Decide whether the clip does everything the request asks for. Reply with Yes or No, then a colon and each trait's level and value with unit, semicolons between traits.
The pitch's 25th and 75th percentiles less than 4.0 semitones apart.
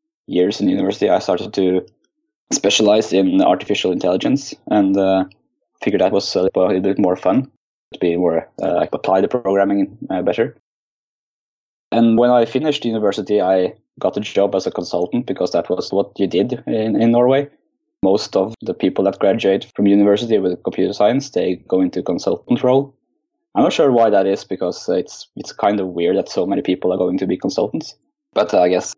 No: average, 4.3 semitones